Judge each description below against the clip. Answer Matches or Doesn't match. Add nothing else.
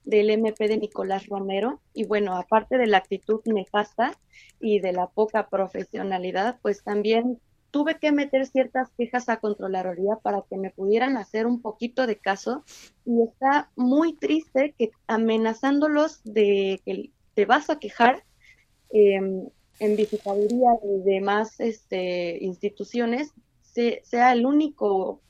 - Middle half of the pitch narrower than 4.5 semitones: Matches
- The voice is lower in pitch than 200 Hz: Doesn't match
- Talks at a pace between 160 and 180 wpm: Doesn't match